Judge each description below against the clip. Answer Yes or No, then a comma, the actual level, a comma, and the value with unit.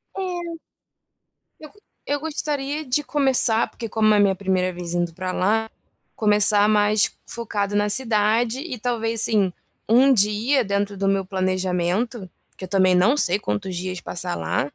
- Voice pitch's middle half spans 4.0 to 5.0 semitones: Yes, average, 4.6 semitones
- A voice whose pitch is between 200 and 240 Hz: Yes, high, 210 Hz